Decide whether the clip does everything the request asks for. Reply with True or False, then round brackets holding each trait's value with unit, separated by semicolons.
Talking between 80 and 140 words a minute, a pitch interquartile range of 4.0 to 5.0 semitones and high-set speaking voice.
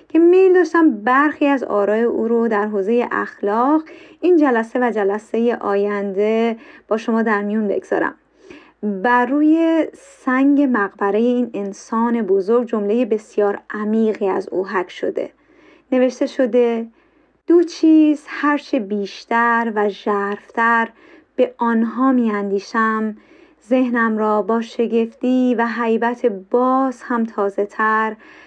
True (120 wpm; 4.5 semitones; 235 Hz)